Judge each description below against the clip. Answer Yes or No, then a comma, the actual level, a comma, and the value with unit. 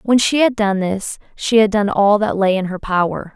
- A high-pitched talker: Yes, high, 205 Hz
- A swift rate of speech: Yes, fast, 250 wpm